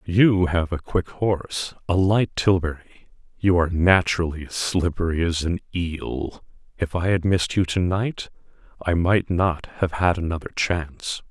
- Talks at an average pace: Yes, average, 160 wpm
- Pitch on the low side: Yes, very low, 90 Hz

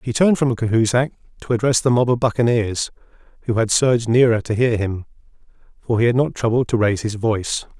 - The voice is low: Yes, low, 115 Hz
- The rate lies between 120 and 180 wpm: No, average, 200 wpm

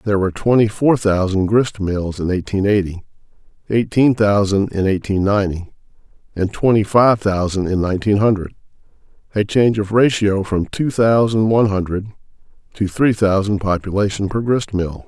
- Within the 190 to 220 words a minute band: No, average, 150 wpm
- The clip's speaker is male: Yes, male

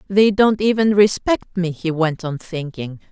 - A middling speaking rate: Yes, average, 175 wpm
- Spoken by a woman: Yes, female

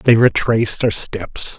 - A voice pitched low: Yes, low, 110 Hz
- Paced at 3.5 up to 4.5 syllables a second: Yes, 3.9 syllables/s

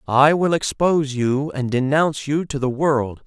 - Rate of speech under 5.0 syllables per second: Yes, 4.5 syllables/s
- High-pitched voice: No, medium, 140 Hz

